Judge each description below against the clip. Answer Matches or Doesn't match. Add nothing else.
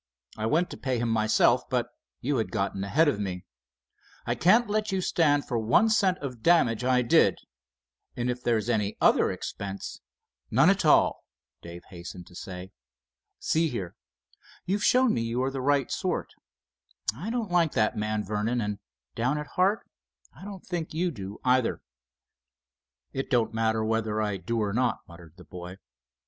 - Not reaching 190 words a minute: Matches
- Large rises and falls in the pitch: Matches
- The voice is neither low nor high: Doesn't match